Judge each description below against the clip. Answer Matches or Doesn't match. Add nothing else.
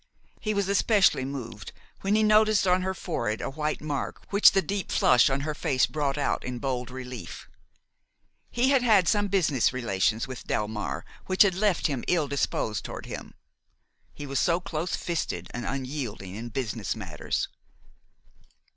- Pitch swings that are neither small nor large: Doesn't match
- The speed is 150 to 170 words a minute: Matches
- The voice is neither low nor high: Matches